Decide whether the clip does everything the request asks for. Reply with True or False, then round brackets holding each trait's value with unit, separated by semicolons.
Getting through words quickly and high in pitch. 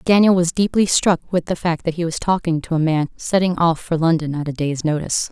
False (250 wpm; 165 Hz)